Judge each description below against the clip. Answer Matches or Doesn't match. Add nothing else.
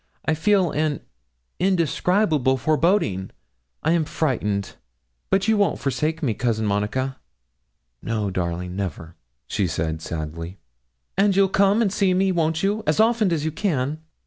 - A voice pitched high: Doesn't match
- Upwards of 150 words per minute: Doesn't match